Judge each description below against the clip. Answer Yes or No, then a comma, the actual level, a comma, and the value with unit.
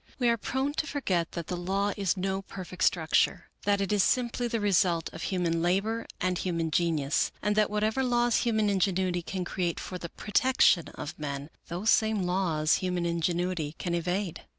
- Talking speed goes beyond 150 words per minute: Yes, average, 180 wpm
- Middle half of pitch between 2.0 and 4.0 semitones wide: Yes, average, 3.4 semitones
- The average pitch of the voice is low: No, medium, 185 Hz